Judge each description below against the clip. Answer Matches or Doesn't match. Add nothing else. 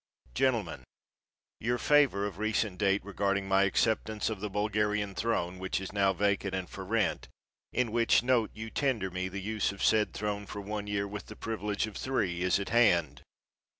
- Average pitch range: Doesn't match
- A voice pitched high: Doesn't match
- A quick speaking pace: Doesn't match